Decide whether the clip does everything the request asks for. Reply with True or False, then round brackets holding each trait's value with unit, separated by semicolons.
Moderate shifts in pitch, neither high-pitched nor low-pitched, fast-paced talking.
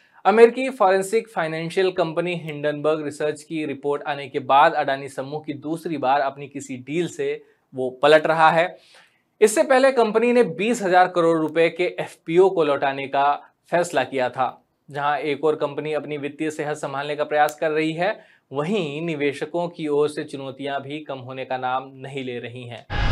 False (3.5 semitones; 150 Hz; 175 wpm)